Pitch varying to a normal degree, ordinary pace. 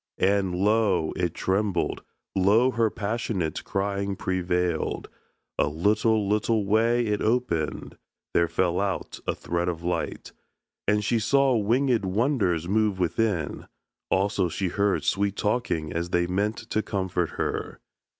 No: average, 3.5 semitones; slow, 130 wpm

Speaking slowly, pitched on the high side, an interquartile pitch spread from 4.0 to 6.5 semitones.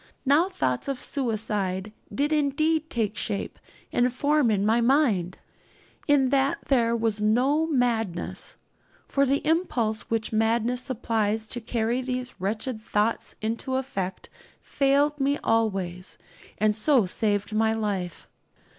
Yes: slow, 130 wpm; high, 230 Hz; average, 4.3 semitones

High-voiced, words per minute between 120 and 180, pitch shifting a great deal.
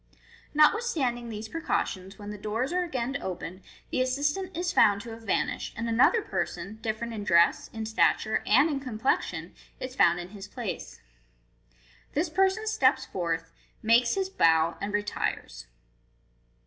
Yes: high, 230 Hz; average, 150 wpm; wide, 6.1 semitones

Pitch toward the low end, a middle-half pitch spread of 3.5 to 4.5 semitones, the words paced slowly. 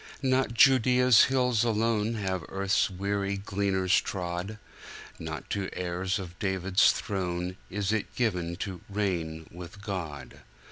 No: low, 100 Hz; average, 3.0 semitones; slow, 120 wpm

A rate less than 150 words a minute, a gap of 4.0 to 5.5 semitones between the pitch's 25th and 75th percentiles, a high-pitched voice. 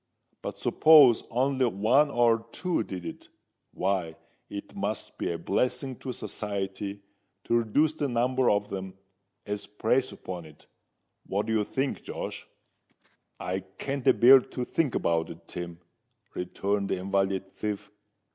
No: average, 140 wpm; average, 4.8 semitones; low, 105 Hz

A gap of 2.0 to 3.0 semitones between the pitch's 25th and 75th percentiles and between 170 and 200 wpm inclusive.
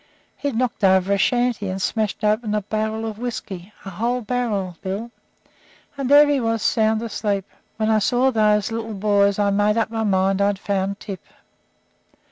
Yes: narrow, 2.4 semitones; average, 175 wpm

